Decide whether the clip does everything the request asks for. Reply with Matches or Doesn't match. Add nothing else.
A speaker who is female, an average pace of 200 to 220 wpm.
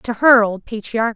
Matches